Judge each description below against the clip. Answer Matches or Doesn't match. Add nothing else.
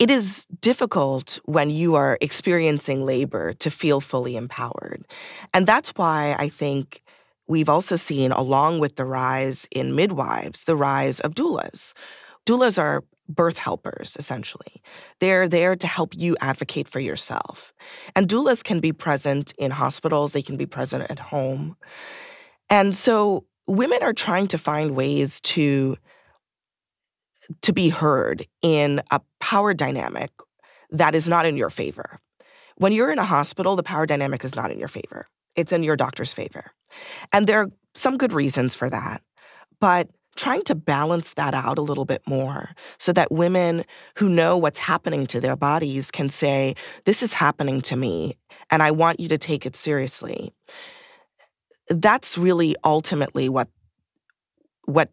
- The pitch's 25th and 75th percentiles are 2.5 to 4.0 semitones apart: Doesn't match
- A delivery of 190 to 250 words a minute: Doesn't match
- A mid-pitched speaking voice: Matches